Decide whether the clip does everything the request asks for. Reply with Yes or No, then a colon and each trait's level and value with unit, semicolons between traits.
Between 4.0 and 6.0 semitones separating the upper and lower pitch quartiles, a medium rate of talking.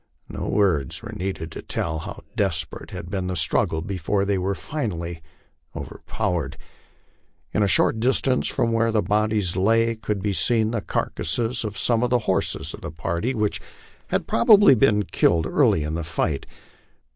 Yes: average, 5.1 semitones; average, 170 wpm